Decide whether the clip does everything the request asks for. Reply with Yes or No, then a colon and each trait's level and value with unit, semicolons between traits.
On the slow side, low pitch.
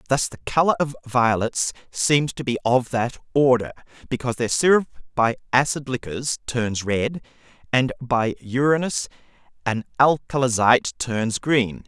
Yes: slow, 130 wpm; low, 125 Hz